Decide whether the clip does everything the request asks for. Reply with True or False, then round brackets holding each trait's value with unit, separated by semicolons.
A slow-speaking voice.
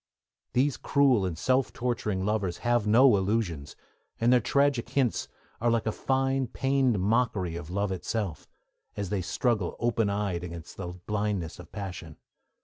False (150 wpm)